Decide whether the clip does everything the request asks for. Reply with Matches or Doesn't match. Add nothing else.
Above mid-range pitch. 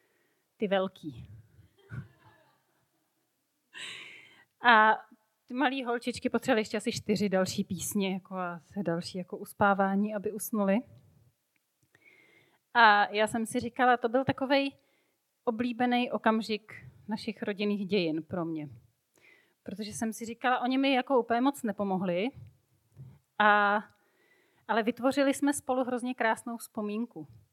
Matches